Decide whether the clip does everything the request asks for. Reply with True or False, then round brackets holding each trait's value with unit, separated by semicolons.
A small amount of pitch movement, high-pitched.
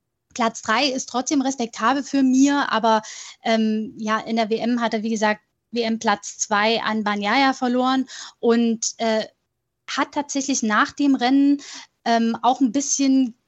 False (3.2 semitones; 235 Hz)